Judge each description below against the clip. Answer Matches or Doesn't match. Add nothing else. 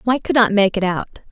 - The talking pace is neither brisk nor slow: Doesn't match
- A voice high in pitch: Matches